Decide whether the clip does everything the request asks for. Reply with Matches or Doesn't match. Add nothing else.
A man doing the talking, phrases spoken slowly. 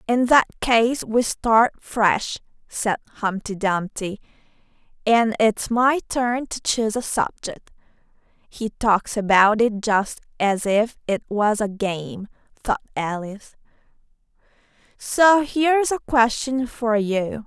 Doesn't match